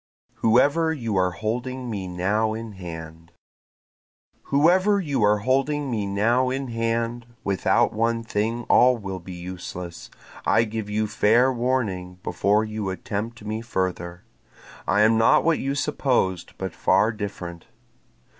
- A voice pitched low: Yes, low, 110 Hz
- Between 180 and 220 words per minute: No, slow, 135 wpm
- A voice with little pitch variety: No, average, 4.4 semitones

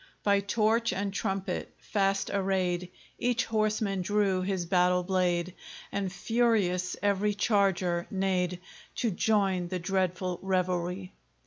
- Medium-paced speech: No, slow, 115 wpm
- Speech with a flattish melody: Yes, narrow, 2.0 semitones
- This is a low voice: No, high, 190 Hz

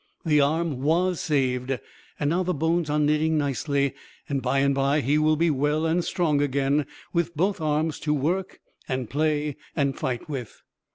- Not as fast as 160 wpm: No, average, 170 wpm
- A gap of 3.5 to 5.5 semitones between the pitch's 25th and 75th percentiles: No, narrow, 2.5 semitones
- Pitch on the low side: No, medium, 150 Hz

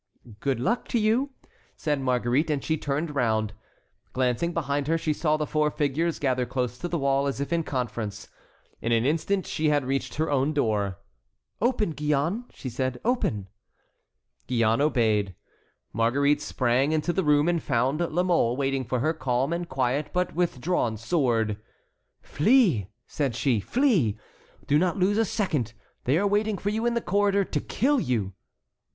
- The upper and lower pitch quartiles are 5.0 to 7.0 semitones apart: Yes, wide, 5.6 semitones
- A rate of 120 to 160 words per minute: No, average, 170 wpm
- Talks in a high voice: No, medium, 145 Hz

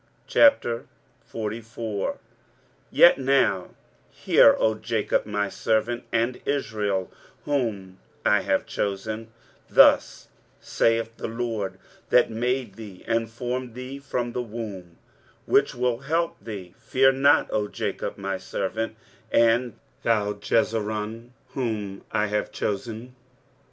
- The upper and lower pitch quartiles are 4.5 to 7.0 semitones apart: No, average, 2.9 semitones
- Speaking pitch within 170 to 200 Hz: No, low, 115 Hz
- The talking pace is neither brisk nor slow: No, slow, 115 wpm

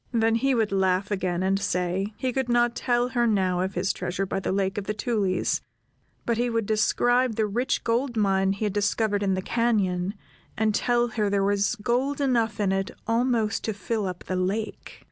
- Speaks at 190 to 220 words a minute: Yes, average, 200 wpm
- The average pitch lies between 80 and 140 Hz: No, high, 210 Hz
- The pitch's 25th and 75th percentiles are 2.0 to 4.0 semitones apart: Yes, average, 3.5 semitones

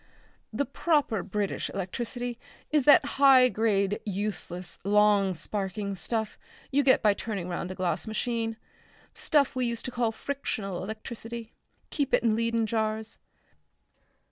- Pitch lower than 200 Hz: No, high, 220 Hz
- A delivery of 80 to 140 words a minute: Yes, slow, 135 wpm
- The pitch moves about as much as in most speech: Yes, average, 3.4 semitones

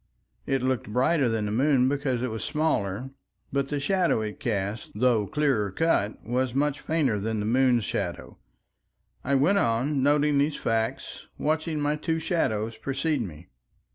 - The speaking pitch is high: No, low, 130 Hz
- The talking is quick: No, average, 160 wpm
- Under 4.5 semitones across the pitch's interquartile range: No, average, 4.9 semitones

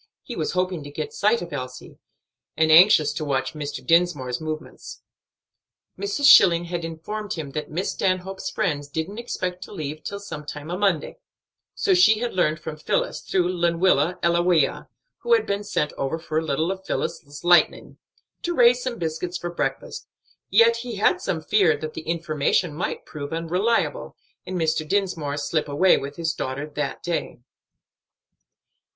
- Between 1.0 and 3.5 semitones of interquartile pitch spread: No, average, 4.0 semitones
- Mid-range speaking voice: Yes, medium, 170 Hz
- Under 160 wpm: No, average, 165 wpm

